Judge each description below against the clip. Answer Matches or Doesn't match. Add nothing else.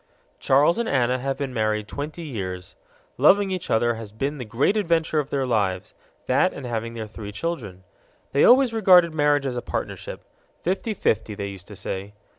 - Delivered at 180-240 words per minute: Matches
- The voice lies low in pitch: Matches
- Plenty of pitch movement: Matches